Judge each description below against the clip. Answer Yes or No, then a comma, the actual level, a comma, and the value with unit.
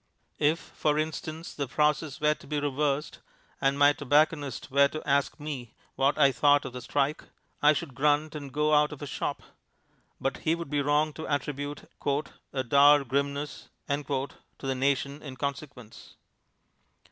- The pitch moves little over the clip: Yes, narrow, 1.5 semitones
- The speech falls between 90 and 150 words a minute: No, average, 160 wpm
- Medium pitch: Yes, medium, 145 Hz